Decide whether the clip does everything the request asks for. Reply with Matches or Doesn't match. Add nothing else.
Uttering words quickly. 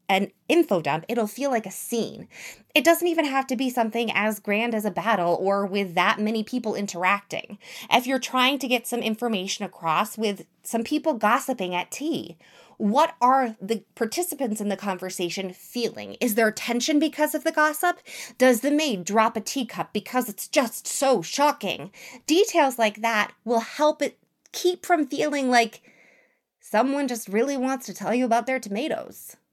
Doesn't match